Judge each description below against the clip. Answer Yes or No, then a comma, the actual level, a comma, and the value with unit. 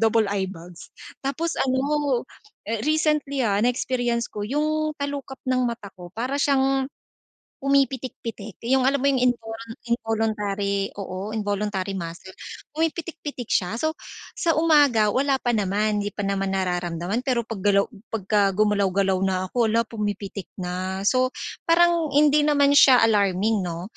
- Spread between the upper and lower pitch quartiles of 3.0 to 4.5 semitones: No, wide, 5.6 semitones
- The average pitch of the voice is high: Yes, high, 225 Hz